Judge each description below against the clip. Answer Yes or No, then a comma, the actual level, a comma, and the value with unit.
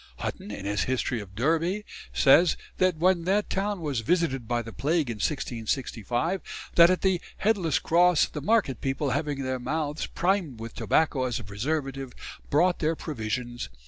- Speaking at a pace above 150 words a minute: Yes, average, 165 wpm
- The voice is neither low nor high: Yes, medium, 145 Hz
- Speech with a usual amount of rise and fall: No, wide, 6.1 semitones